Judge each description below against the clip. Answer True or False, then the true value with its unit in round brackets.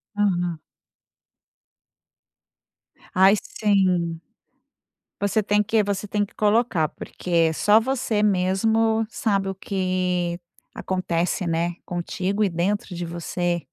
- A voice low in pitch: False (190 Hz)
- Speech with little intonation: False (3.0 semitones)